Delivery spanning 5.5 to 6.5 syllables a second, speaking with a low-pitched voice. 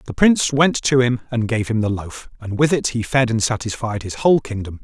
Yes: 5.6 syllables/s; low, 120 Hz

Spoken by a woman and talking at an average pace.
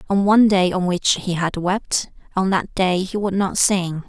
No: female; fast, 220 wpm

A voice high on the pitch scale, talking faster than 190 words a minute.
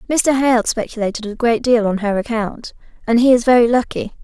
Yes: high, 230 Hz; average, 200 wpm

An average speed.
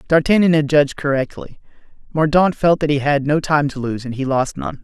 No: fast, 210 wpm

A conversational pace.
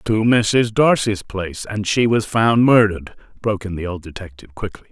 Yes: average, 185 wpm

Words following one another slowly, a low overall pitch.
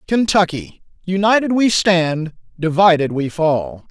No: slow, 90 wpm; medium, 180 Hz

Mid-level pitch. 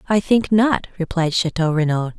Yes: medium, 180 Hz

